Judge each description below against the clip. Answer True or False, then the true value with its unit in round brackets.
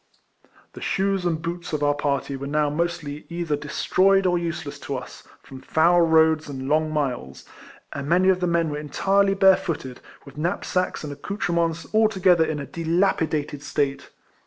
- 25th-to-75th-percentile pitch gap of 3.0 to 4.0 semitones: True (3.4 semitones)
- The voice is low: False (160 Hz)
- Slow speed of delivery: False (165 wpm)